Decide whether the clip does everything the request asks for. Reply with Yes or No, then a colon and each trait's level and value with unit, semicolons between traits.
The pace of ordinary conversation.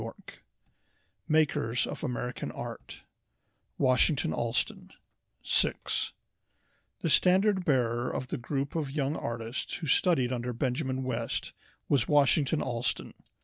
No: slow, 110 wpm